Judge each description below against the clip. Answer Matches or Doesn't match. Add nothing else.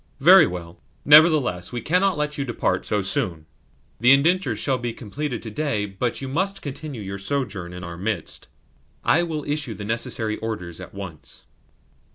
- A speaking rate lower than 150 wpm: Doesn't match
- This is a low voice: Matches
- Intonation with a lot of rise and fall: Matches